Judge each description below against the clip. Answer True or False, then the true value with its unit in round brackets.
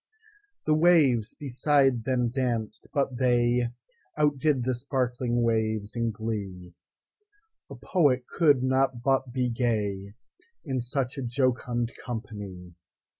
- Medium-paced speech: False (100 wpm)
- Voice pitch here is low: True (125 Hz)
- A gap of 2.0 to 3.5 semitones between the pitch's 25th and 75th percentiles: True (2.8 semitones)